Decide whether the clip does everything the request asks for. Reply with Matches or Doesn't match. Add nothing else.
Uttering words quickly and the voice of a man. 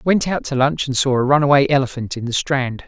Matches